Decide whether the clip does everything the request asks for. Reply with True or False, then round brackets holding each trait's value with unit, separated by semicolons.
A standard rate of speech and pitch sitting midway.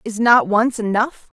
False (175 wpm; 225 Hz)